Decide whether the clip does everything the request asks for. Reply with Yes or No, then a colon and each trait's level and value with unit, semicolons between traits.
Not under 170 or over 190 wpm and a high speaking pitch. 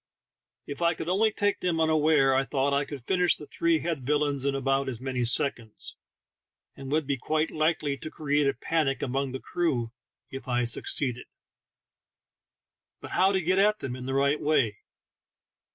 No: average, 175 wpm; medium, 140 Hz